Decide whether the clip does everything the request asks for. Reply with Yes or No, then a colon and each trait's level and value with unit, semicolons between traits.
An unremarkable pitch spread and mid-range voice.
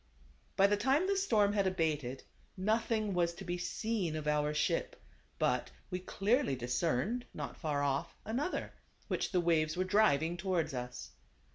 No: wide, 5.7 semitones; medium, 180 Hz